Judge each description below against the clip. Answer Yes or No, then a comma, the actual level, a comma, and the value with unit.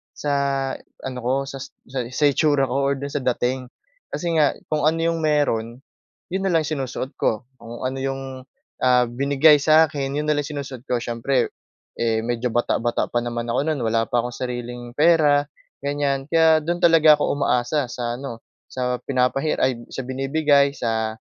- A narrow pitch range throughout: No, average, 3.3 semitones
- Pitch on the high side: No, low, 135 Hz